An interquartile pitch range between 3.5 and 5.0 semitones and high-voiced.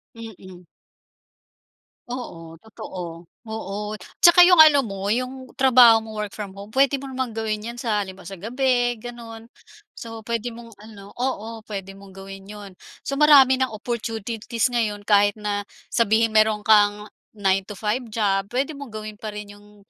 No: average, 2.9 semitones; high, 220 Hz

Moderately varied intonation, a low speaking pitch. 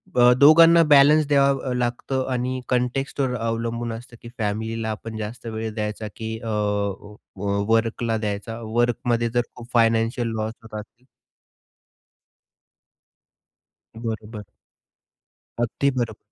No: narrow, 2.1 semitones; low, 115 Hz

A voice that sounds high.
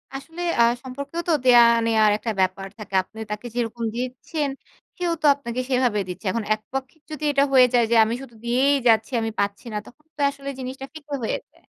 Yes: very high, 250 Hz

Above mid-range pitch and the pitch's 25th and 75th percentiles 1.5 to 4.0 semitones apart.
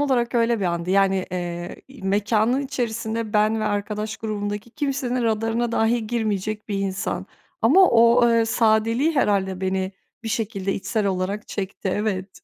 Yes: high, 215 Hz; average, 2.9 semitones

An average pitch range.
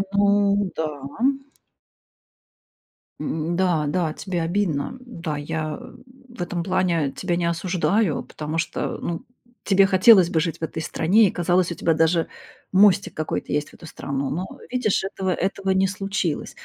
Yes: average, 3.3 semitones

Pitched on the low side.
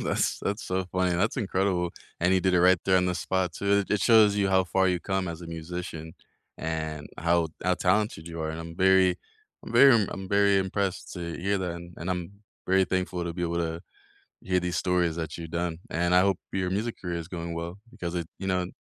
Yes: very low, 90 Hz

